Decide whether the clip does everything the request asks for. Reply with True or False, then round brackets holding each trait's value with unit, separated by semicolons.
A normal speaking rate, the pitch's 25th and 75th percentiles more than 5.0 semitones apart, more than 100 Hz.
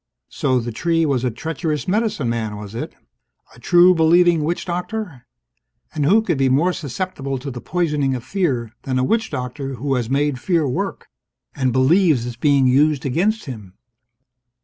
True (170 wpm; 5.4 semitones; 140 Hz)